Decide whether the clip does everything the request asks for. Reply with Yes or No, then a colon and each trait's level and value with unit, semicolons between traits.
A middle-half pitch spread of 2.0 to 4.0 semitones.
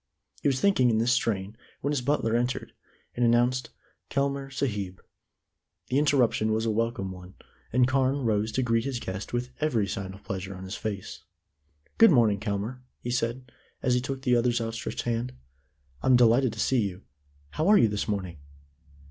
Yes: average, 3.7 semitones